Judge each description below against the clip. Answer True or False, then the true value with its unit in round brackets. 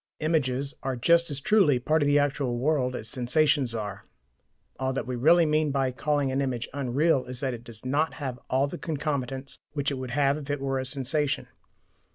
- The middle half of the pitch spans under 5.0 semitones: True (2.6 semitones)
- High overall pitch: False (135 Hz)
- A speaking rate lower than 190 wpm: False (200 wpm)